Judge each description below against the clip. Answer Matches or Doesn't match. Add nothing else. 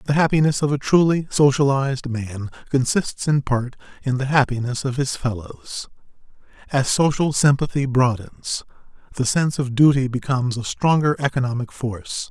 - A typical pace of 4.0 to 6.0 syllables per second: Matches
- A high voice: Doesn't match